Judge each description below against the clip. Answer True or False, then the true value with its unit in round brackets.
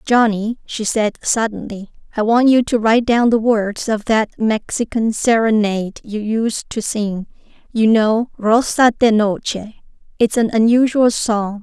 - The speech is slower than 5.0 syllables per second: True (4.2 syllables/s)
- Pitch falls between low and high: False (220 Hz)